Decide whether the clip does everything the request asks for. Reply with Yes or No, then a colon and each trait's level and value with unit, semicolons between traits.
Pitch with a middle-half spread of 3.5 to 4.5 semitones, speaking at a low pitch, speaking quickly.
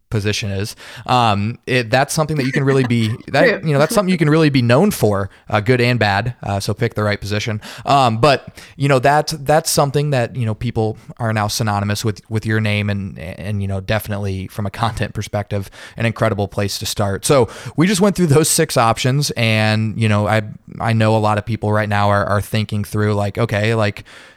Yes: average, 3.8 semitones; low, 110 Hz; fast, 225 wpm